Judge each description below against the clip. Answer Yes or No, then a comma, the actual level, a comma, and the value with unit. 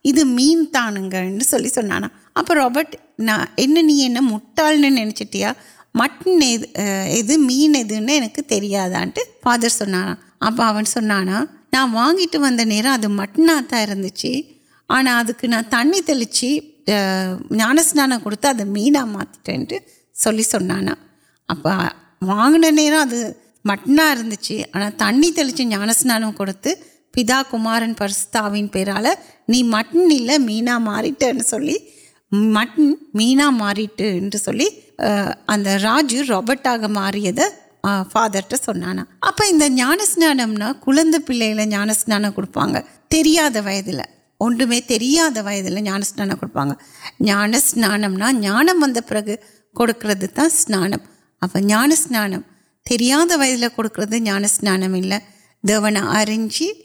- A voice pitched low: No, high, 235 Hz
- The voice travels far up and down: Yes, wide, 5.8 semitones